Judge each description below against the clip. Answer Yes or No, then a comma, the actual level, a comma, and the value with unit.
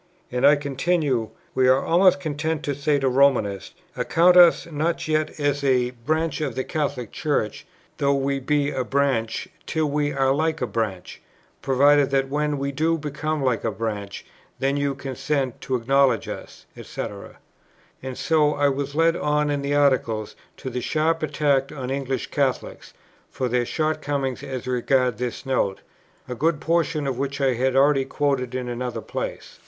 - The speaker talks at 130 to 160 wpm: No, average, 170 wpm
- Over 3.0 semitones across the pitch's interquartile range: No, average, 2.7 semitones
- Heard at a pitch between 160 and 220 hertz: No, medium, 140 Hz